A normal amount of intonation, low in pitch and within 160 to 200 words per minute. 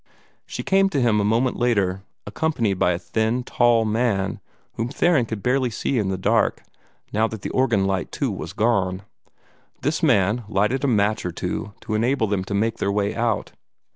Yes: average, 3.4 semitones; low, 110 Hz; average, 190 wpm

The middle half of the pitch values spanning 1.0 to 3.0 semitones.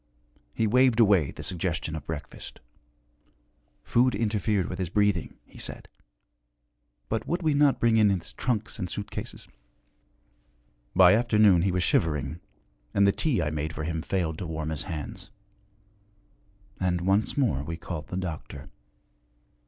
No: average, 5.0 semitones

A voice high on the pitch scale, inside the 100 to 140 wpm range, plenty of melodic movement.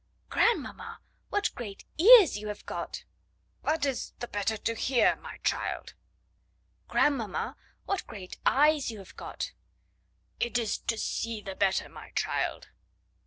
Yes: high, 240 Hz; slow, 135 wpm; wide, 6.9 semitones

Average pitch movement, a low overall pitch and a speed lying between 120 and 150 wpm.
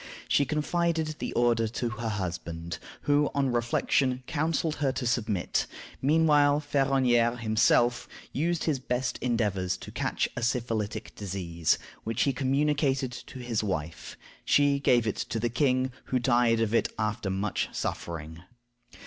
Yes: average, 4.4 semitones; low, 120 Hz; average, 140 wpm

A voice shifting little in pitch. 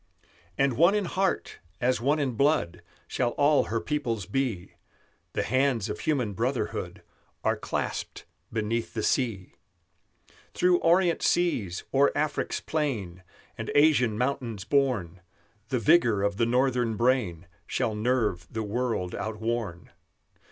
No: average, 5.1 semitones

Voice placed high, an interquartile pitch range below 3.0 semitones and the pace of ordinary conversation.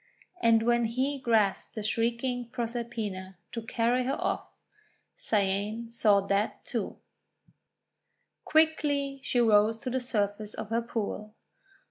No: high, 230 Hz; narrow, 2.6 semitones; slow, 120 wpm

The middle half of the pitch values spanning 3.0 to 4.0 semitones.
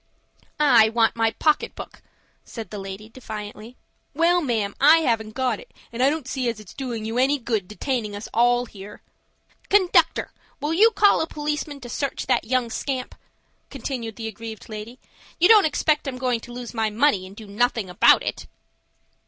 No: average, 4.5 semitones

